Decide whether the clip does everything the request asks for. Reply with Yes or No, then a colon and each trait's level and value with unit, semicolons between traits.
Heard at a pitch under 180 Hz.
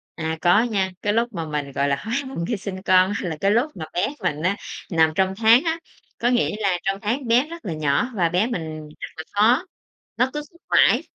No: high, 195 Hz